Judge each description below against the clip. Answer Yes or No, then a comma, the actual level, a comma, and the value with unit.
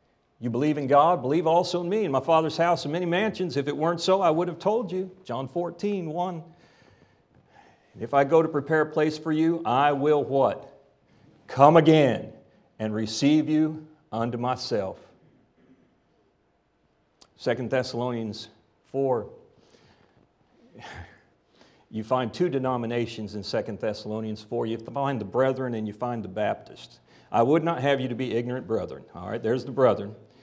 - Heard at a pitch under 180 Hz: Yes, medium, 140 Hz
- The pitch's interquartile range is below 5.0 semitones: No, wide, 5.4 semitones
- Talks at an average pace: Yes, average, 160 wpm